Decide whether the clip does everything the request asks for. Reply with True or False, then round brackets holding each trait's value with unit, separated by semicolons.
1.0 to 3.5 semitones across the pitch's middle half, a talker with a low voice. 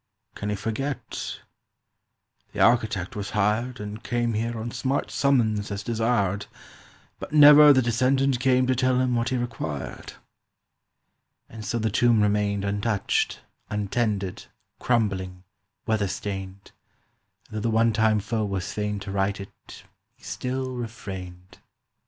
True (3.2 semitones; 110 Hz)